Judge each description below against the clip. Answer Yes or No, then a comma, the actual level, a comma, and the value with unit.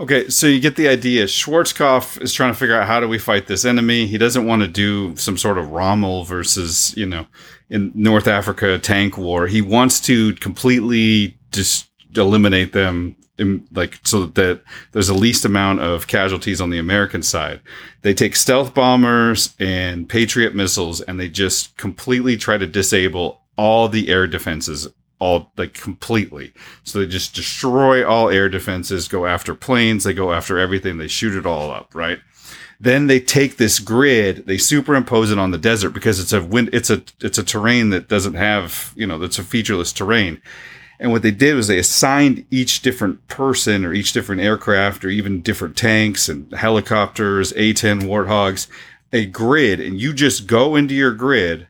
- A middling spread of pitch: Yes, average, 3.9 semitones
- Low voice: Yes, low, 105 Hz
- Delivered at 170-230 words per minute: Yes, average, 185 wpm